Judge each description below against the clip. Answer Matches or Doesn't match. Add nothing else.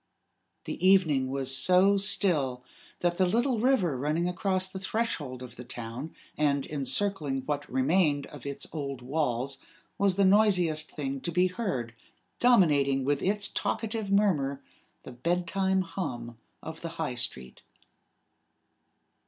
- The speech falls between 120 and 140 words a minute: Matches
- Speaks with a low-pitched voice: Doesn't match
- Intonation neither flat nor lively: Doesn't match